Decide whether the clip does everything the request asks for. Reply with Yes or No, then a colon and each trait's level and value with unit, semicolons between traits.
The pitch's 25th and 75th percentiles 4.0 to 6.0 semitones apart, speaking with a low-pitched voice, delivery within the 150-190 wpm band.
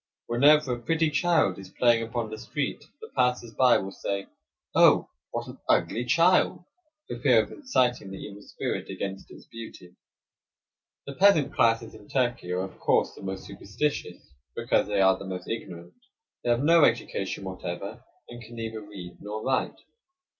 Yes: average, 5.3 semitones; low, 115 Hz; average, 170 wpm